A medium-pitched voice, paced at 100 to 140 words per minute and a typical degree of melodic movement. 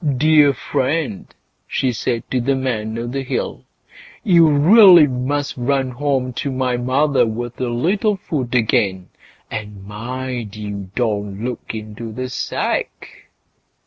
No: low, 125 Hz; slow, 135 wpm; average, 3.9 semitones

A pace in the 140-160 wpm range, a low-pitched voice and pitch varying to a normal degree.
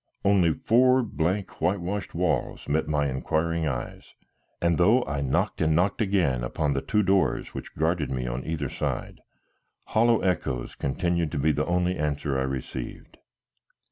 Yes: average, 155 wpm; very low, 80 Hz; average, 4.7 semitones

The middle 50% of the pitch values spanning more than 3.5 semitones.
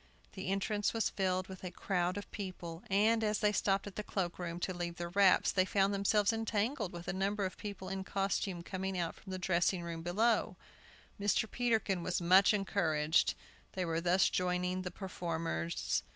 No: narrow, 2.4 semitones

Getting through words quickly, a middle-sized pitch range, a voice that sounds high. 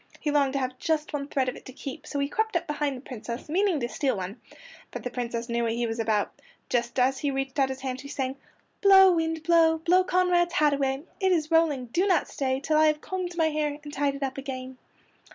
Yes: fast, 245 wpm; average, 3.9 semitones; very high, 280 Hz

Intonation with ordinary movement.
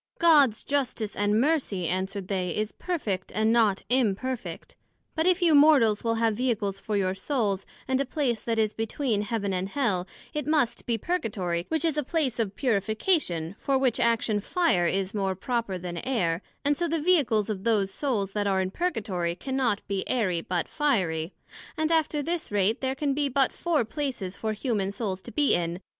No: wide, 6.1 semitones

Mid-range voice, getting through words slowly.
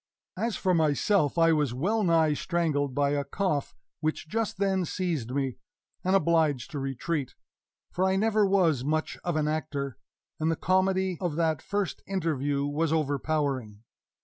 No: medium, 160 Hz; average, 155 wpm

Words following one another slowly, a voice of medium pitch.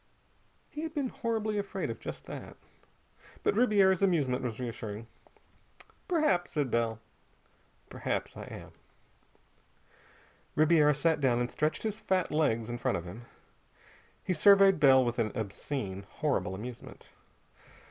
Yes: slow, 130 wpm; medium, 150 Hz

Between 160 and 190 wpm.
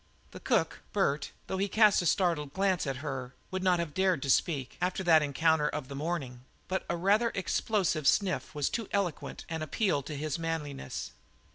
Yes: average, 185 wpm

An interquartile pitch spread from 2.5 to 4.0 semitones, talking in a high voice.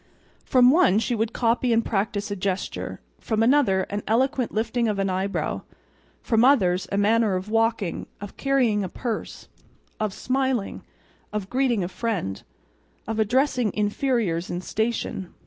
Yes: average, 3.6 semitones; high, 220 Hz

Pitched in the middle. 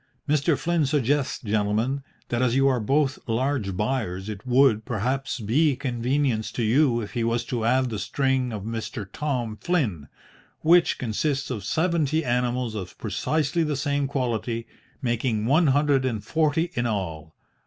No: low, 125 Hz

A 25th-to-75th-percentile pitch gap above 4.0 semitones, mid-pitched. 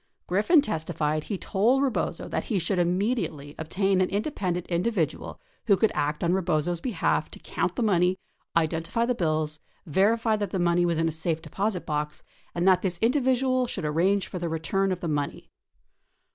Yes: average, 4.4 semitones; medium, 180 Hz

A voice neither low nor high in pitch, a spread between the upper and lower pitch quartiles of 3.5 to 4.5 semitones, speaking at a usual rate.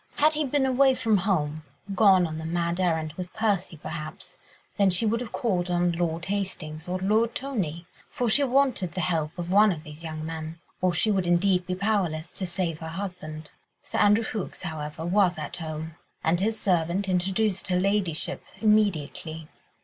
Yes: medium, 180 Hz; average, 4.1 semitones; average, 180 wpm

